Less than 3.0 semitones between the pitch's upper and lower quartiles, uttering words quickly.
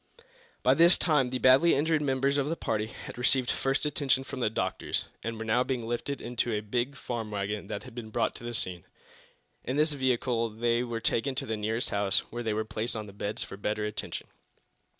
No: average, 3.5 semitones; fast, 210 wpm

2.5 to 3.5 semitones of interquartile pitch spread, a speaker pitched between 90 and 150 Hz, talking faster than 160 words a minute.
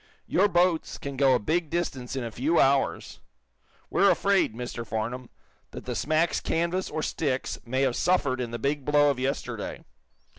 No: average, 4.7 semitones; medium, 140 Hz; average, 175 wpm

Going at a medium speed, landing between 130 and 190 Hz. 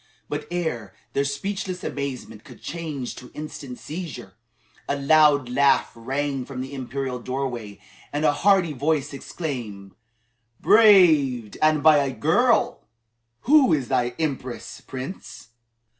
No: slow, 125 wpm; medium, 140 Hz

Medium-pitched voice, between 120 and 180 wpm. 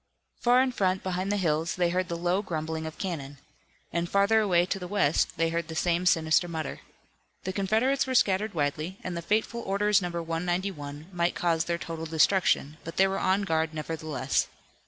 No: medium, 175 Hz; average, 190 wpm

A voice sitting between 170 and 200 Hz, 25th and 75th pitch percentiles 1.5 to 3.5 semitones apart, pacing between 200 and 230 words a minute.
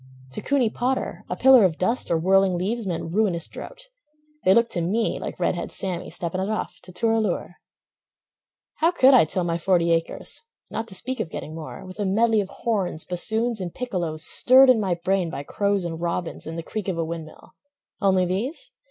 No: high, 190 Hz; average, 4.9 semitones; fast, 205 wpm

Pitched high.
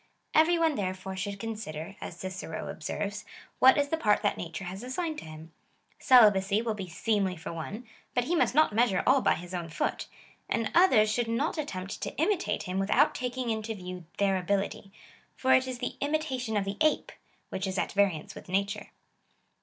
Yes: high, 210 Hz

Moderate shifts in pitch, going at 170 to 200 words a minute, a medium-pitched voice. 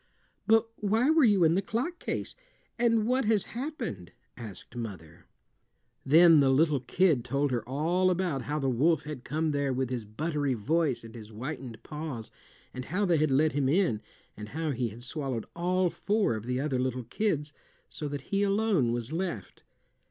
No: wide, 6.5 semitones; average, 185 wpm; medium, 150 Hz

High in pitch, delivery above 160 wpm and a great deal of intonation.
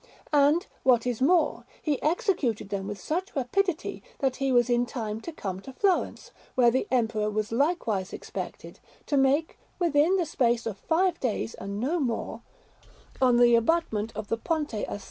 Yes: very high, 255 Hz; average, 175 wpm; wide, 5.9 semitones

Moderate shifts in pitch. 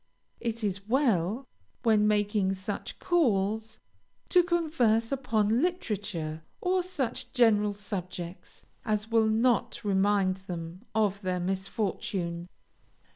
Yes: average, 3.4 semitones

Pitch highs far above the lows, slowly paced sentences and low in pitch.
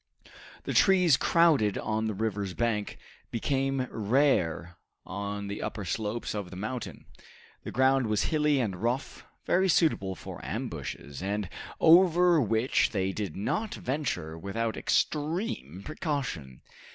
Yes: wide, 6.6 semitones; slow, 130 wpm; low, 110 Hz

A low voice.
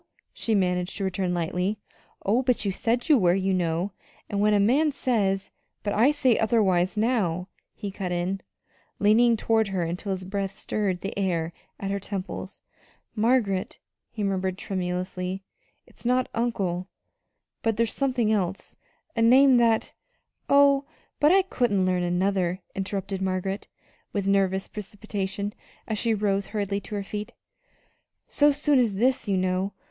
No: high, 200 Hz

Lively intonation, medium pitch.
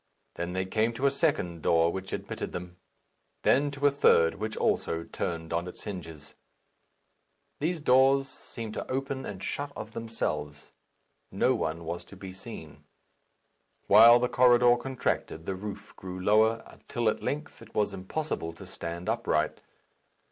No: wide, 6.4 semitones; low, 105 Hz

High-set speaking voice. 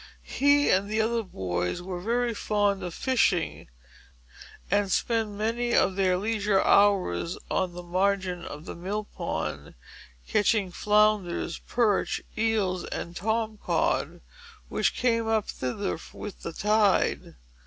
Yes: high, 205 Hz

